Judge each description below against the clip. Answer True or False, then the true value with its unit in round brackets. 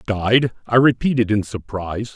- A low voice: True (110 Hz)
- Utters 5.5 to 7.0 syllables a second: False (4.8 syllables/s)